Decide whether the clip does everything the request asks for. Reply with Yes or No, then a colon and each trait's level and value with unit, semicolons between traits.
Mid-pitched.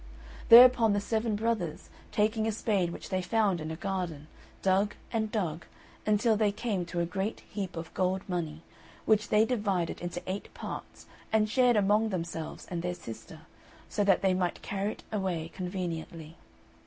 No: high, 195 Hz